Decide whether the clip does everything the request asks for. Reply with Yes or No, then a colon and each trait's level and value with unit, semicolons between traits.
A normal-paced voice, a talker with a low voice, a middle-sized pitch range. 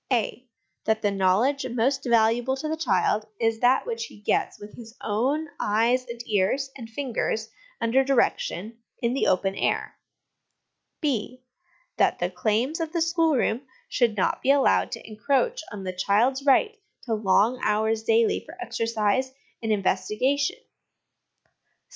No: average, 145 wpm; high, 235 Hz; average, 4.0 semitones